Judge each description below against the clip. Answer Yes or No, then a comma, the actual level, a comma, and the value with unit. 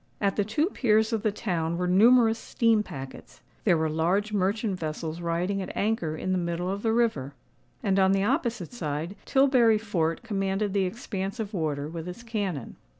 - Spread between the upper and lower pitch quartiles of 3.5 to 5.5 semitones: Yes, average, 4.7 semitones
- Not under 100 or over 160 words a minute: No, average, 175 wpm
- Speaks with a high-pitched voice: Yes, high, 195 Hz